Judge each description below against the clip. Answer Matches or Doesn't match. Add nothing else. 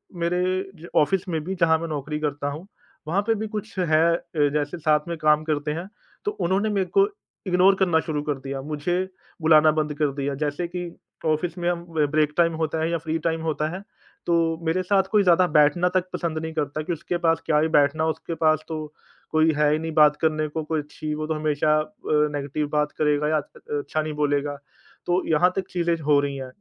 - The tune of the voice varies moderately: Doesn't match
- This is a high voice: Doesn't match